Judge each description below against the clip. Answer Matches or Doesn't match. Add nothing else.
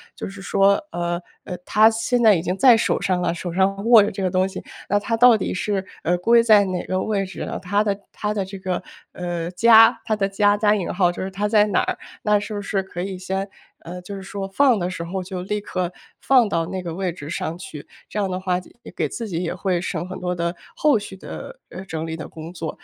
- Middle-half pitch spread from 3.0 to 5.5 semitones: Doesn't match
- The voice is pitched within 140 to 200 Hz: Matches